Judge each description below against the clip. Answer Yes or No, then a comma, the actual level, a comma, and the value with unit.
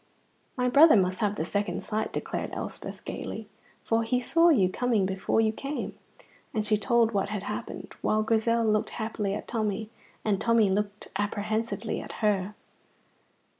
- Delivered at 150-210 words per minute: Yes, average, 160 wpm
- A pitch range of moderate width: No, narrow, 2.2 semitones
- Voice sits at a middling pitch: No, high, 215 Hz